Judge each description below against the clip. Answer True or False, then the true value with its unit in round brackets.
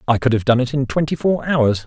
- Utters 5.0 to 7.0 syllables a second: True (6.0 syllables/s)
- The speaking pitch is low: True (130 Hz)